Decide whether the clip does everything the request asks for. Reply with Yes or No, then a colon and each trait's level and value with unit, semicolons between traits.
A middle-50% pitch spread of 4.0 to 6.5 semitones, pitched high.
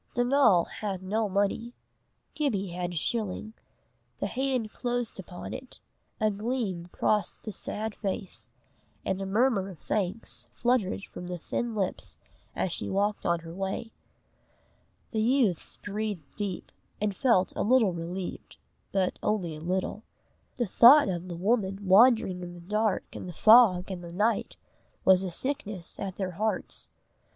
No: average, 3.6 semitones; high, 200 Hz